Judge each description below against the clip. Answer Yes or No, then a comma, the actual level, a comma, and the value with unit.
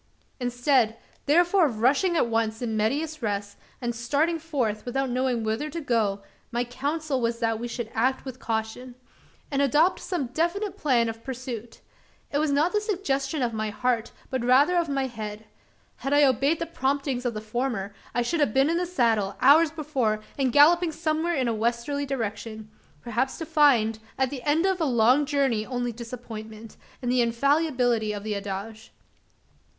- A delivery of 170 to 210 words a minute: Yes, average, 175 wpm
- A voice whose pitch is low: No, very high, 255 Hz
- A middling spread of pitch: Yes, average, 4.5 semitones